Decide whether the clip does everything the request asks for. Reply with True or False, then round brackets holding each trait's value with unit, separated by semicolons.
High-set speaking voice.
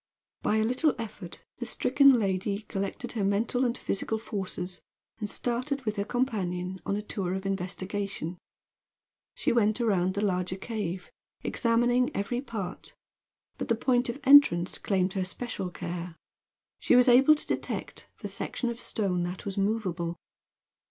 True (205 Hz)